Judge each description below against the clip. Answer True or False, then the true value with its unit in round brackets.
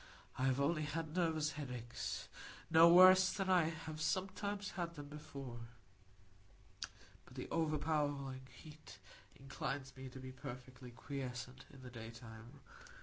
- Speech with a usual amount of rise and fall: True (4.0 semitones)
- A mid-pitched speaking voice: True (145 Hz)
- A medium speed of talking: False (125 wpm)